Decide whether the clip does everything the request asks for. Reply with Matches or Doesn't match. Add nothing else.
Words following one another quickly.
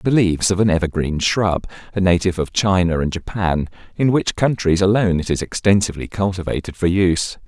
Doesn't match